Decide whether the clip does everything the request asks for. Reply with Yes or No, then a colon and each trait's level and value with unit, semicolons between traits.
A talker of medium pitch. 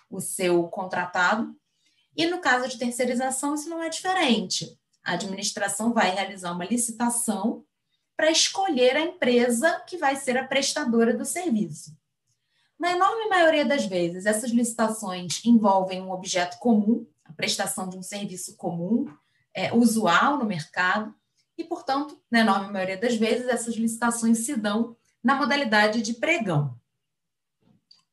No: high, 230 Hz